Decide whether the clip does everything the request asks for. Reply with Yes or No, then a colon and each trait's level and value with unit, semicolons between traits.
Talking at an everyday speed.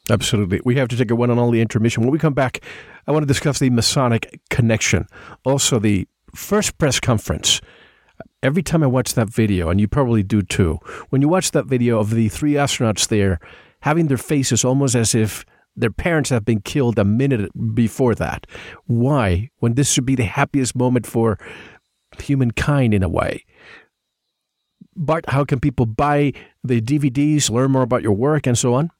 Yes: average, 190 wpm